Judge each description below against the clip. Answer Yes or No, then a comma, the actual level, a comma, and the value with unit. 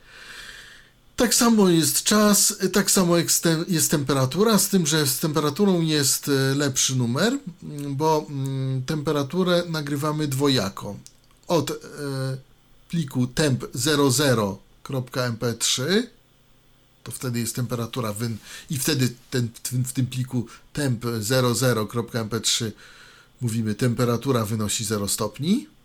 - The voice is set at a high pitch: No, low, 135 Hz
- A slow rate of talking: Yes, slow, 95 wpm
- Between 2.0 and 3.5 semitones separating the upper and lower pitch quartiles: No, average, 4.4 semitones